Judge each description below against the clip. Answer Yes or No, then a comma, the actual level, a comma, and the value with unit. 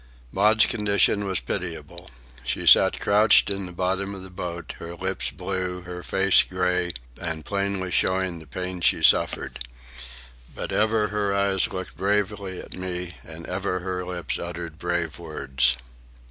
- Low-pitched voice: Yes, very low, 95 Hz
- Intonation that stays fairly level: Yes, narrow, 2.1 semitones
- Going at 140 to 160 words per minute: Yes, average, 150 wpm